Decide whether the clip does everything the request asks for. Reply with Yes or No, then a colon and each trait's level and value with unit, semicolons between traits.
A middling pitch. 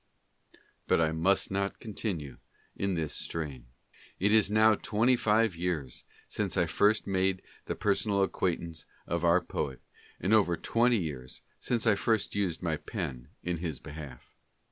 No: very low, 90 Hz